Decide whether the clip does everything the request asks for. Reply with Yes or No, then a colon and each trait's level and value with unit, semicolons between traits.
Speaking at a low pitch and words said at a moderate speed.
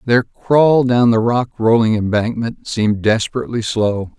Yes: low, 115 Hz; average, 145 wpm